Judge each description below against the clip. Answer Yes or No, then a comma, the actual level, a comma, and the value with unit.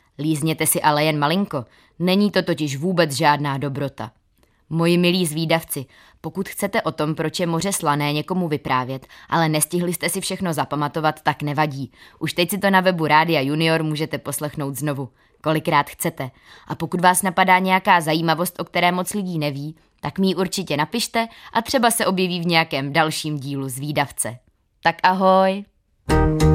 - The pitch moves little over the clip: No, average, 3.8 semitones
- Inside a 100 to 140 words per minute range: No, average, 165 wpm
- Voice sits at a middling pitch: Yes, medium, 160 Hz